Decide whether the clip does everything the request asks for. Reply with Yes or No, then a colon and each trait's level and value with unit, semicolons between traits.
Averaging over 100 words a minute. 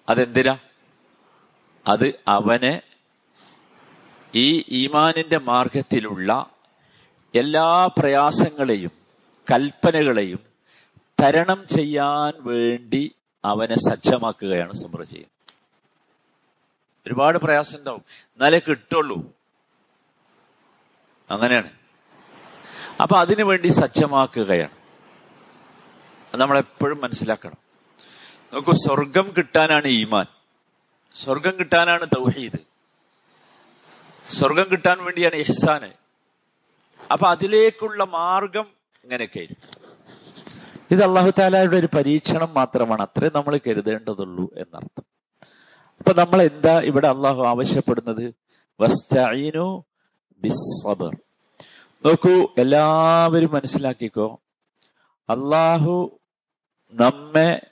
No: slow, 60 wpm